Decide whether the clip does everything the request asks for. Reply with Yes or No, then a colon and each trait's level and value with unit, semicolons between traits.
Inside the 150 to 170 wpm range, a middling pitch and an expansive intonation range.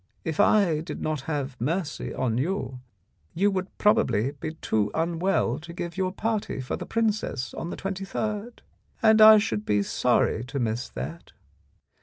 Yes: average, 160 wpm; medium, 165 Hz; wide, 7.5 semitones